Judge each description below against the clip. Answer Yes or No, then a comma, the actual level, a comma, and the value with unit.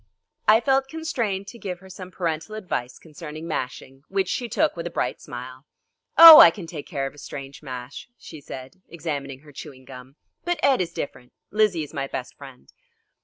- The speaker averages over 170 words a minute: Yes, average, 190 wpm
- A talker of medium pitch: Yes, medium, 160 Hz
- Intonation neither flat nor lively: No, wide, 6.4 semitones